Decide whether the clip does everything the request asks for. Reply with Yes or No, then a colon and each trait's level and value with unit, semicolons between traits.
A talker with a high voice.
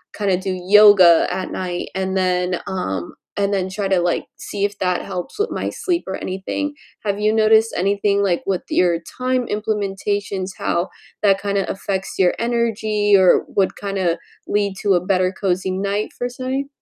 Yes: high, 195 Hz